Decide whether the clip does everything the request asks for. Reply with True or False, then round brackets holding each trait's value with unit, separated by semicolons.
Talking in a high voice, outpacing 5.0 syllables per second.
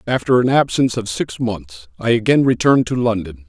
False (115 Hz; 5.6 syllables/s)